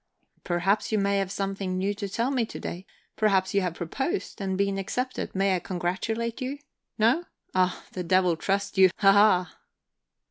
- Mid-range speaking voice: No, high, 195 Hz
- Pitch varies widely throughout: No, average, 2.7 semitones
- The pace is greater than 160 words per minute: Yes, average, 170 wpm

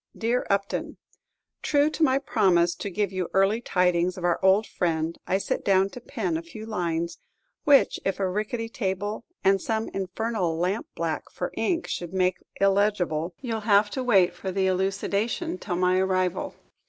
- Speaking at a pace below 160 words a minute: No, average, 170 wpm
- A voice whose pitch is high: Yes, high, 195 Hz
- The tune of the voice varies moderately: Yes, average, 3.3 semitones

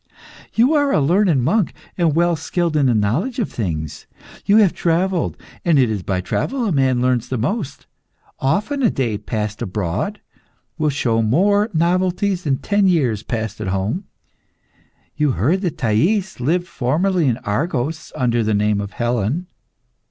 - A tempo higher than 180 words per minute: No, average, 165 wpm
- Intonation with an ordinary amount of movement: No, wide, 8.4 semitones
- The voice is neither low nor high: Yes, medium, 145 Hz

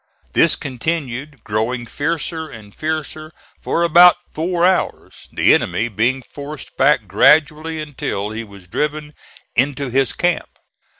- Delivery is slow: Yes, slow, 125 wpm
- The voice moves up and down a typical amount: Yes, average, 5.0 semitones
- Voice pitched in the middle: Yes, medium, 145 Hz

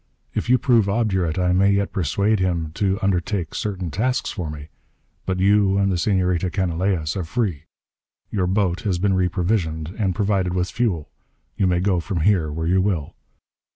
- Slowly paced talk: No, average, 175 wpm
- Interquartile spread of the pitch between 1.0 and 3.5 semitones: Yes, narrow, 2.5 semitones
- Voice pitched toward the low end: Yes, very low, 95 Hz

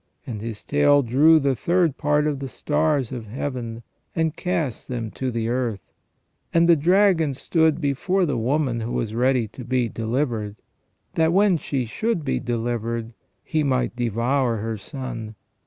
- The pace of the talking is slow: No, average, 160 wpm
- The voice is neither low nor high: No, low, 130 Hz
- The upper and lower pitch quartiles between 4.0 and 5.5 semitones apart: Yes, average, 4.7 semitones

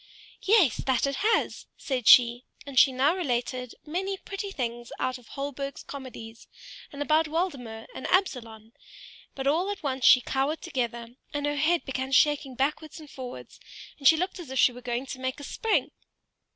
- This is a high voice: Yes, very high, 270 Hz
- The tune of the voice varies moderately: Yes, average, 3.9 semitones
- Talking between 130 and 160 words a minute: No, average, 175 wpm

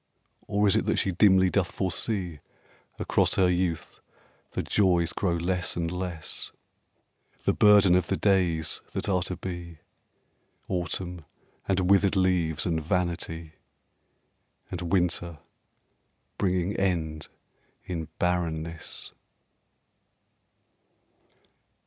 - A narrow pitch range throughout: Yes, narrow, 1.9 semitones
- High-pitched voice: No, very low, 90 Hz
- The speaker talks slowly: Yes, slow, 105 wpm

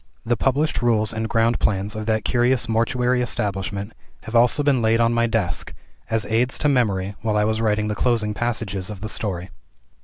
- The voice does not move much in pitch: Yes, narrow, 2.3 semitones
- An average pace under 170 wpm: No, average, 190 wpm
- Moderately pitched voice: No, low, 110 Hz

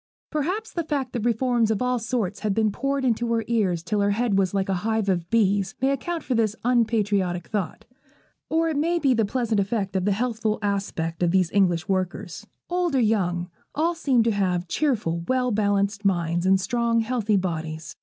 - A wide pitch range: No, average, 4.5 semitones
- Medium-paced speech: Yes, average, 195 wpm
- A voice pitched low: No, high, 215 Hz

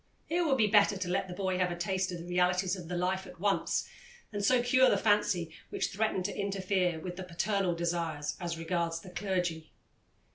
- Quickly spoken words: Yes, fast, 210 wpm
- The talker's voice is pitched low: No, medium, 185 Hz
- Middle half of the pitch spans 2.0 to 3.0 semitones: Yes, narrow, 2.4 semitones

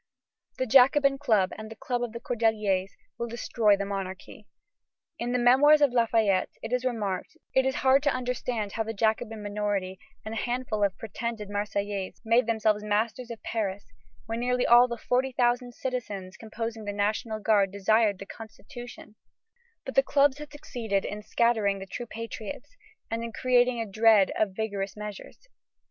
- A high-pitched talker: Yes, high, 225 Hz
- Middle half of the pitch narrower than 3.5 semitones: Yes, average, 3.1 semitones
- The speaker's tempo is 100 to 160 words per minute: No, average, 170 wpm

